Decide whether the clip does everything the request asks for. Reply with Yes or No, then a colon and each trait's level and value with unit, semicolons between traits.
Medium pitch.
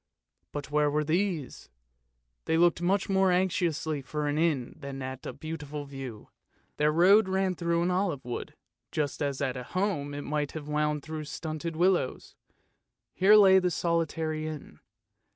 Yes: medium, 155 Hz